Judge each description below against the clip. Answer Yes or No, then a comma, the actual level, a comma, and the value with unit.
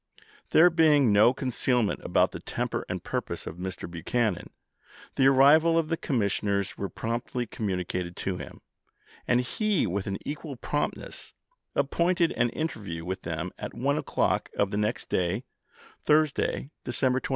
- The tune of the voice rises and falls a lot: Yes, wide, 7.1 semitones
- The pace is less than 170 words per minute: Yes, average, 155 wpm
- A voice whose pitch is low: Yes, low, 120 Hz